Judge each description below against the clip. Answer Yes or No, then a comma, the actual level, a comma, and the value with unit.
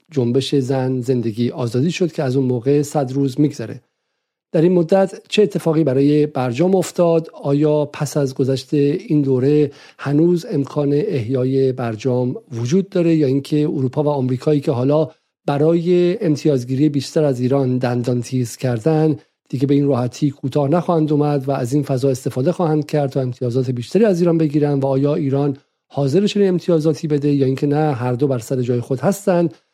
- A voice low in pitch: No, medium, 145 Hz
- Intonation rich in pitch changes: No, average, 3.1 semitones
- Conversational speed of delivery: No, fast, 170 wpm